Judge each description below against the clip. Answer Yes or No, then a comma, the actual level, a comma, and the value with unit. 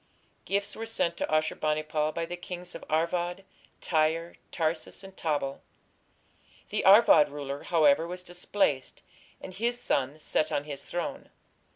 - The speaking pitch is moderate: Yes, medium, 165 Hz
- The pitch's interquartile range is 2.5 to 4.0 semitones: Yes, average, 2.9 semitones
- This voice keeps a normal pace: Yes, average, 150 wpm